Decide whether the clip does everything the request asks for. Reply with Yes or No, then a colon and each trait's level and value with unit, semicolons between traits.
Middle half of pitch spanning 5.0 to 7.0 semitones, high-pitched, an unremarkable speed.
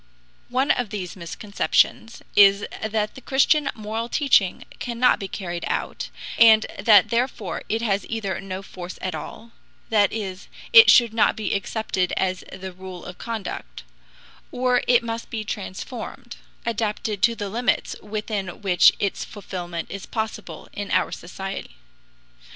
No: average, 3.3 semitones; high, 210 Hz; average, 145 wpm